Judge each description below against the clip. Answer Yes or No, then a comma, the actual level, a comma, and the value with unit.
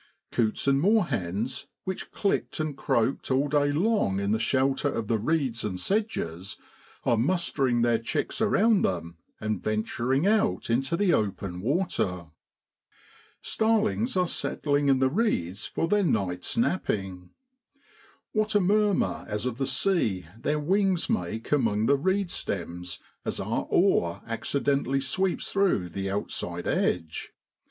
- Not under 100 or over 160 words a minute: Yes, average, 140 wpm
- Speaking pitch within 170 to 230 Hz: No, low, 135 Hz